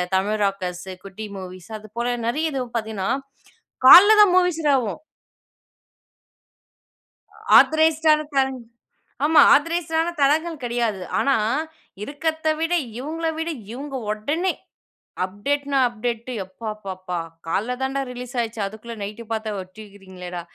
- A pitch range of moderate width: No, wide, 6.8 semitones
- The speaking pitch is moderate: No, high, 240 Hz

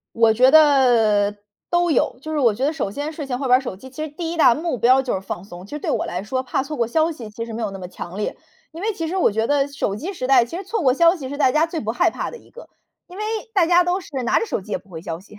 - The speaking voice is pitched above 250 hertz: Yes, very high, 265 Hz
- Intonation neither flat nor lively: No, wide, 6.4 semitones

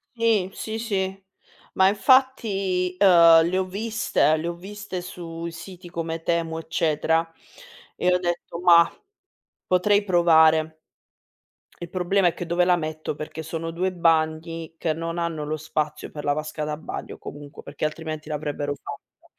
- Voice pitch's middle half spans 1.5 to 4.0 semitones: Yes, average, 2.7 semitones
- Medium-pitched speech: Yes, medium, 170 Hz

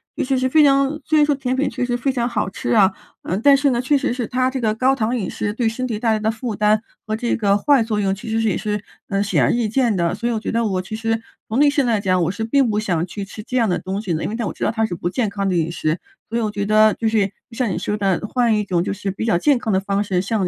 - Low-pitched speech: No, high, 220 Hz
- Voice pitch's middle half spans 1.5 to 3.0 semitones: No, average, 3.7 semitones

